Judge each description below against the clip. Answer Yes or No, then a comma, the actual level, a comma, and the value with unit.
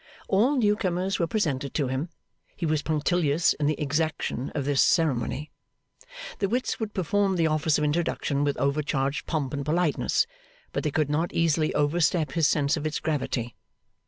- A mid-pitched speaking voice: Yes, medium, 155 Hz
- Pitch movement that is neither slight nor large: Yes, average, 3.2 semitones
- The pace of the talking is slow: No, average, 170 wpm